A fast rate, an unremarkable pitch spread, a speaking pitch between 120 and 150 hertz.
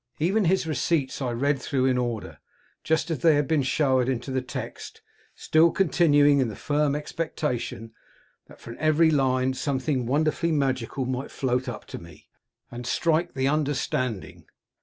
No: average, 160 wpm; average, 3.4 semitones; medium, 140 Hz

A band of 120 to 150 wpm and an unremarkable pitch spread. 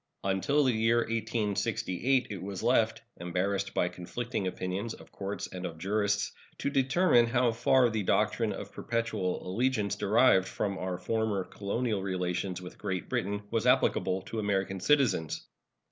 Yes: average, 145 wpm; average, 3.8 semitones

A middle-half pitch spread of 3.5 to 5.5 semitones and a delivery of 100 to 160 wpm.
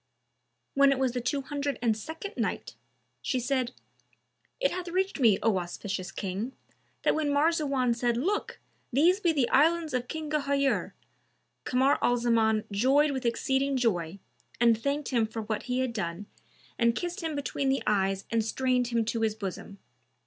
No: average, 4.2 semitones; average, 170 wpm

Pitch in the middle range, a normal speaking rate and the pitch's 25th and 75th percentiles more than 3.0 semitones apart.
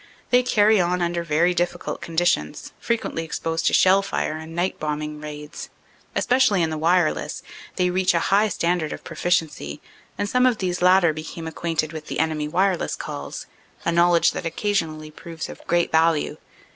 No: medium, 170 Hz; average, 175 wpm; narrow, 2.6 semitones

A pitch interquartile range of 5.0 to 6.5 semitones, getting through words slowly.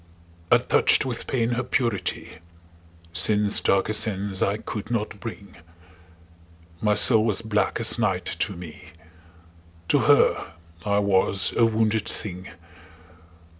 No: narrow, 2.4 semitones; slow, 125 wpm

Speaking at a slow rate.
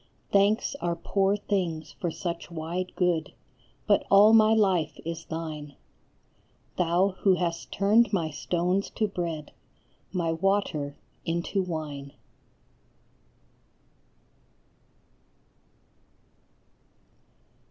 Yes: slow, 90 wpm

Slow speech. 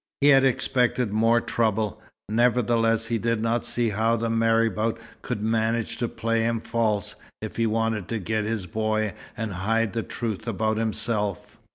No: average, 165 wpm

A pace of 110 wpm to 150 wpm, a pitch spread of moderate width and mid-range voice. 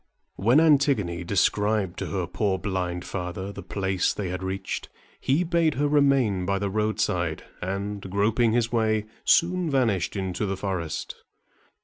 No: average, 145 wpm; average, 4.4 semitones; low, 100 Hz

